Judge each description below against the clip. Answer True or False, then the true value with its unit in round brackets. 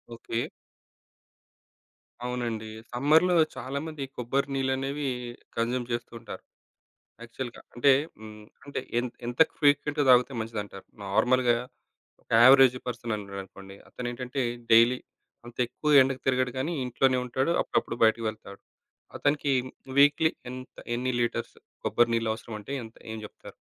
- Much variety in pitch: False (2.8 semitones)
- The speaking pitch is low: True (125 Hz)